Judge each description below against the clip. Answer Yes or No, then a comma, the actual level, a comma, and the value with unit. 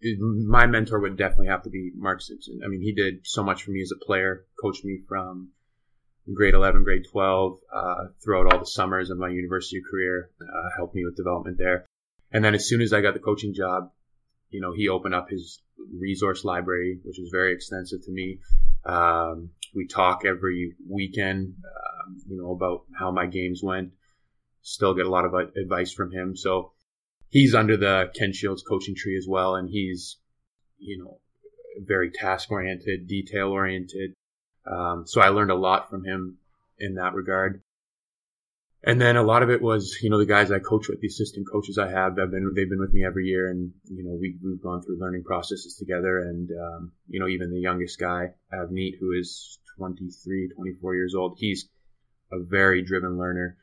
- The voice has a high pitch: No, very low, 95 Hz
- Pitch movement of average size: No, narrow, 1.5 semitones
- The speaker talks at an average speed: Yes, average, 190 wpm